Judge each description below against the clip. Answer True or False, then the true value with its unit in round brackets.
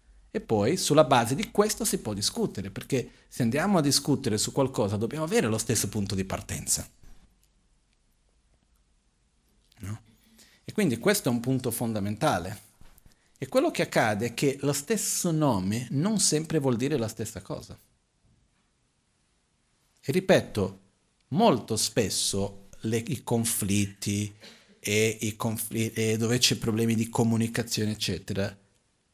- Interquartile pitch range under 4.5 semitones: False (5.1 semitones)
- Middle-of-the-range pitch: False (115 Hz)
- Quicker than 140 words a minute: False (130 wpm)